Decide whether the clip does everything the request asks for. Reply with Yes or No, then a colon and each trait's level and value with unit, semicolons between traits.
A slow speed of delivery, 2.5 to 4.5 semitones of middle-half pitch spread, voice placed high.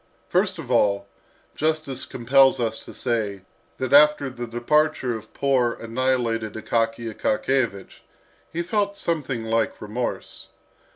No: slow, 120 wpm; average, 4.1 semitones; low, 125 Hz